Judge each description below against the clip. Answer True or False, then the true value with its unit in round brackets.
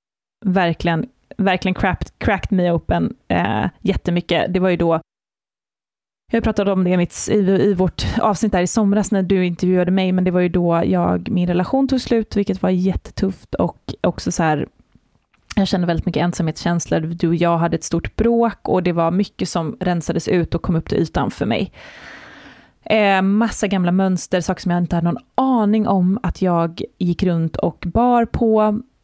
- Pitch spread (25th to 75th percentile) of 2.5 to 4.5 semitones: True (2.9 semitones)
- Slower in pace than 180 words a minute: False (185 wpm)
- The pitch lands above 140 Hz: True (185 Hz)